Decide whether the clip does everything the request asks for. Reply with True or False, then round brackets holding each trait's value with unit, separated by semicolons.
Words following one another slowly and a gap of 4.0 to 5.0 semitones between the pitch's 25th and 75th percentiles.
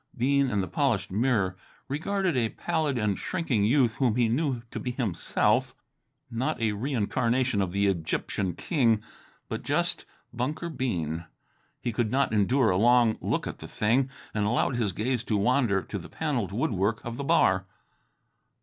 False (165 wpm; 4.6 semitones)